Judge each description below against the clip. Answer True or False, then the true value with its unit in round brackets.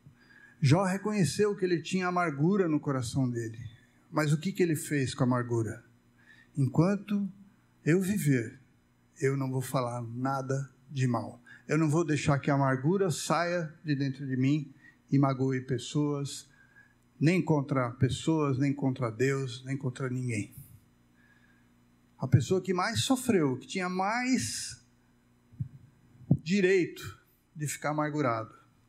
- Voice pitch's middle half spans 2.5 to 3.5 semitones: False (4.5 semitones)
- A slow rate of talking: False (135 wpm)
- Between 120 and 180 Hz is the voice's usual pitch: True (140 Hz)